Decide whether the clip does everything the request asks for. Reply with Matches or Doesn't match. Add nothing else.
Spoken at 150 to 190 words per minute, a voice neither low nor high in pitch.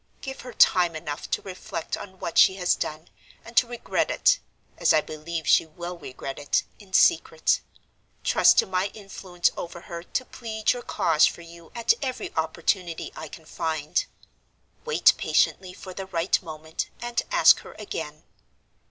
Matches